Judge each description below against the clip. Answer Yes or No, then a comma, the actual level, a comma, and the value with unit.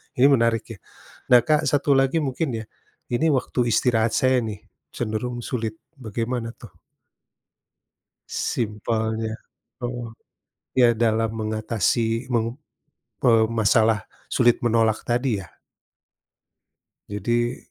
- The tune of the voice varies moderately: No, narrow, 1.9 semitones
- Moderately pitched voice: No, low, 115 Hz